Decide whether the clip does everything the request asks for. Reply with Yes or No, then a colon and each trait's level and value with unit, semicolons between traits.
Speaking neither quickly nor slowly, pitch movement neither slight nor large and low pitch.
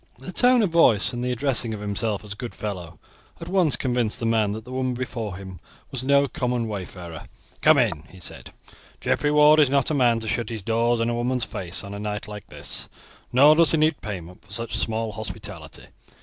No: fast, 215 wpm; average, 4.3 semitones; low, 115 Hz